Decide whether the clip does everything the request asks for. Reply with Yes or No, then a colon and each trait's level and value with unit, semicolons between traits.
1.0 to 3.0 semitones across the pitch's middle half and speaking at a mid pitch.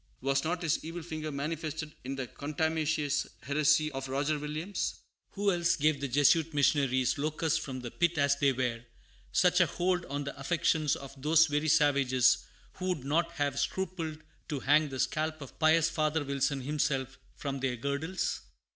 Yes: narrow, 2.6 semitones; medium, 150 Hz